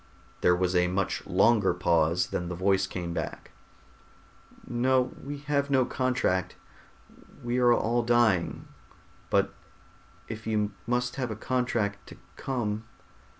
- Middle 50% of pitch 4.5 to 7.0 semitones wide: Yes, average, 5.0 semitones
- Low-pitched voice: Yes, low, 110 Hz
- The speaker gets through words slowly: Yes, slow, 130 wpm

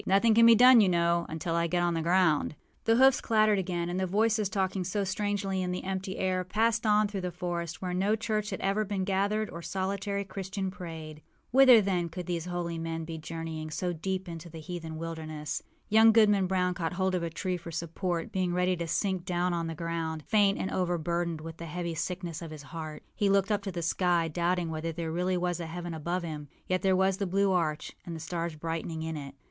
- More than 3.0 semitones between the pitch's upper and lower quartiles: No, average, 2.7 semitones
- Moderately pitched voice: Yes, medium, 180 Hz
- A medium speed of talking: No, fast, 225 wpm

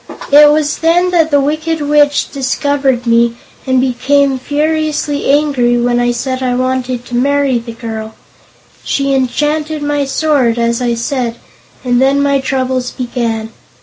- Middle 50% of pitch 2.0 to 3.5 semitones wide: Yes, average, 3.2 semitones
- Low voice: No, very high, 265 Hz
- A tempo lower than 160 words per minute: Yes, average, 150 wpm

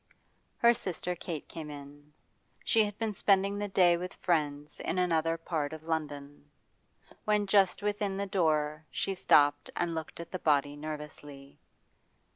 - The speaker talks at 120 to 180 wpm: Yes, average, 150 wpm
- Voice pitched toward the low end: No, medium, 165 Hz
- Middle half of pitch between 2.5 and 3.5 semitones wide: No, average, 4.5 semitones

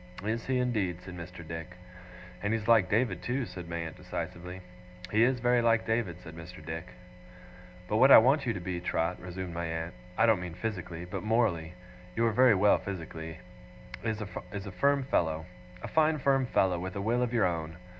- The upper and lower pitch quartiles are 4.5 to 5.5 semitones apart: Yes, average, 5.1 semitones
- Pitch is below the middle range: Yes, very low, 95 Hz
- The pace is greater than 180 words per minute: Yes, average, 200 wpm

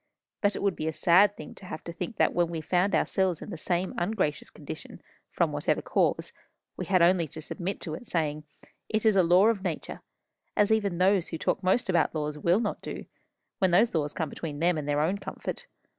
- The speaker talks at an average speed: No, fast, 220 wpm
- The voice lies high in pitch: No, medium, 175 Hz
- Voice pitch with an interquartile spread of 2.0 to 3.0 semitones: No, average, 3.7 semitones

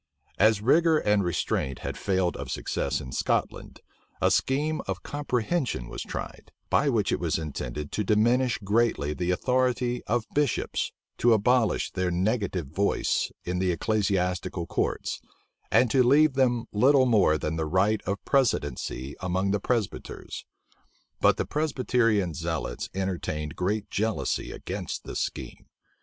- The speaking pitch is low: Yes, low, 105 Hz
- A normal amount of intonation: No, wide, 5.7 semitones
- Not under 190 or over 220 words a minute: No, average, 140 wpm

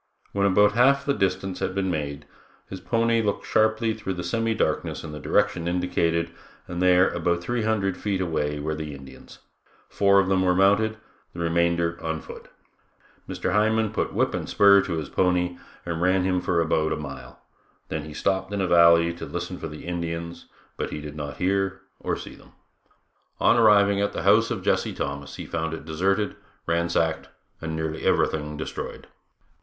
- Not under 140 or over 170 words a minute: No, average, 185 wpm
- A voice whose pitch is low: Yes, very low, 90 Hz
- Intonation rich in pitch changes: No, average, 3.4 semitones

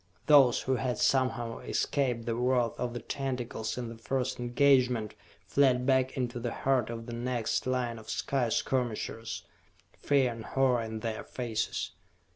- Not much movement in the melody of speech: Yes, narrow, 2.1 semitones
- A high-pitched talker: No, low, 125 Hz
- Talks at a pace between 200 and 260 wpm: No, average, 155 wpm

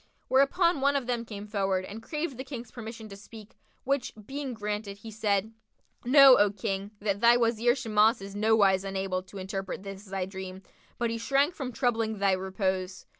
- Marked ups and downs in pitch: No, average, 3.7 semitones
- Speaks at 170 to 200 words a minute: Yes, average, 180 wpm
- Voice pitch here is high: Yes, high, 215 Hz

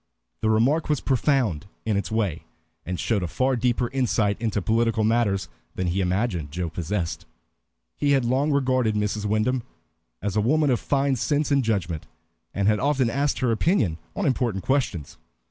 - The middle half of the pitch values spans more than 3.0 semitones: Yes, average, 5.0 semitones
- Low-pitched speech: Yes, low, 115 Hz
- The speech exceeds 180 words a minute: No, average, 170 wpm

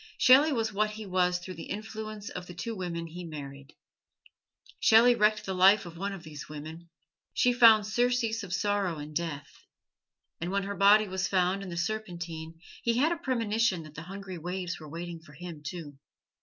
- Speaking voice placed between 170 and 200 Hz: Yes, medium, 185 Hz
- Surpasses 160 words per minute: Yes, average, 190 wpm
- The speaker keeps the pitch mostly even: No, average, 4.3 semitones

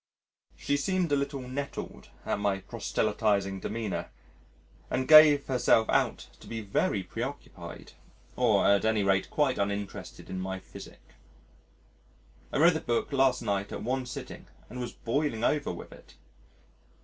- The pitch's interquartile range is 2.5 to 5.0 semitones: No, wide, 5.6 semitones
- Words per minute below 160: Yes, average, 145 wpm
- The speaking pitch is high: No, low, 115 Hz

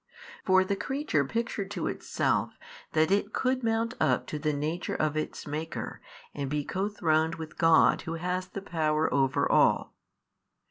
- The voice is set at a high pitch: No, medium, 165 Hz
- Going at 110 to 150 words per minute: No, average, 165 wpm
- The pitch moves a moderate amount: Yes, average, 4.4 semitones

